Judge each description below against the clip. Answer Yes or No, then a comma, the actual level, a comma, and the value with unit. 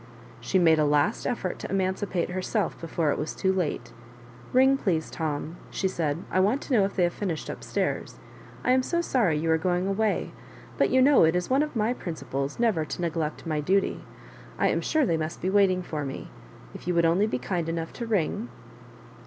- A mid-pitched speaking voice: Yes, medium, 180 Hz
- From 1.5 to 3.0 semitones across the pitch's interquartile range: No, average, 4.4 semitones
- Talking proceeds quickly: Yes, fast, 225 wpm